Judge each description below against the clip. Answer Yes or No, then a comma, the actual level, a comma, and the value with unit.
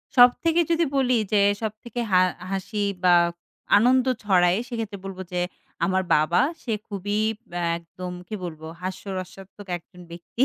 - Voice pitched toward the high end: Yes, high, 195 Hz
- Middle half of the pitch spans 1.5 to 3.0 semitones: No, average, 4.2 semitones